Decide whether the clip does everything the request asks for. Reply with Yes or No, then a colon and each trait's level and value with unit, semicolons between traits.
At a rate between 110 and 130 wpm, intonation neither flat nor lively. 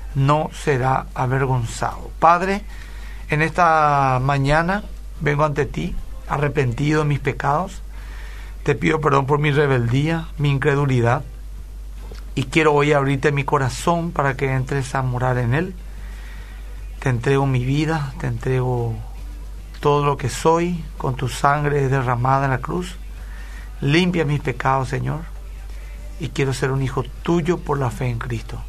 No: average, 140 wpm; average, 3.1 semitones